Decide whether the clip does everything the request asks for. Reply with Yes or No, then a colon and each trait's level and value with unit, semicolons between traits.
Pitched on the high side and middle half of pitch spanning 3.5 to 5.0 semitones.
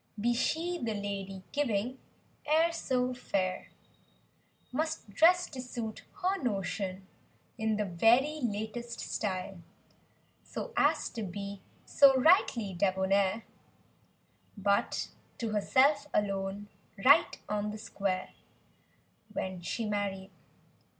Yes: high, 215 Hz; average, 4.7 semitones